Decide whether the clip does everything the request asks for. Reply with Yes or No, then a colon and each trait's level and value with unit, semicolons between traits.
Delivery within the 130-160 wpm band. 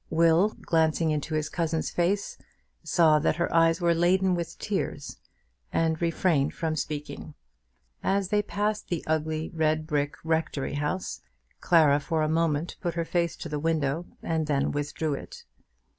Yes: average, 155 wpm